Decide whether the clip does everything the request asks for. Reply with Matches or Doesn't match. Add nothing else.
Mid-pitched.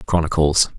Doesn't match